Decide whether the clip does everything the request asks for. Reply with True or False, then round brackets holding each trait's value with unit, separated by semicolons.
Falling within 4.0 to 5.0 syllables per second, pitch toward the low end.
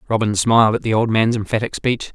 False (6.2 syllables/s; 110 Hz)